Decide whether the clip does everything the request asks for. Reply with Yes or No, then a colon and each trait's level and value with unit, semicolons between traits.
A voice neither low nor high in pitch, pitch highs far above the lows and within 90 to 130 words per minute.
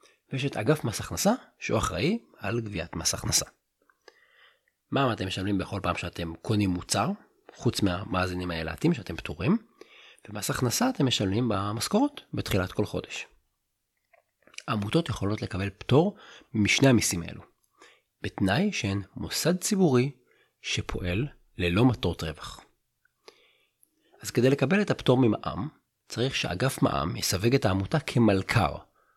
No: low, 110 Hz; wide, 6.4 semitones; average, 125 wpm